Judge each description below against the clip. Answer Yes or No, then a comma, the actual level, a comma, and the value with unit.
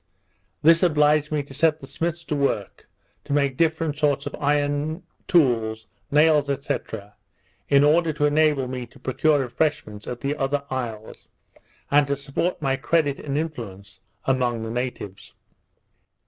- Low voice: No, medium, 145 Hz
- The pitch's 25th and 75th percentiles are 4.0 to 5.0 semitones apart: No, average, 2.9 semitones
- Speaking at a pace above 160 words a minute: No, average, 145 wpm